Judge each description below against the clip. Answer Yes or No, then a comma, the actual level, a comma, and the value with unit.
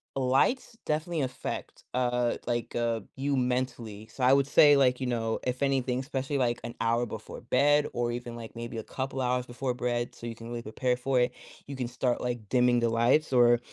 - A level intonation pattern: Yes, narrow, 1.9 semitones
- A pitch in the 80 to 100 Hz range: No, low, 125 Hz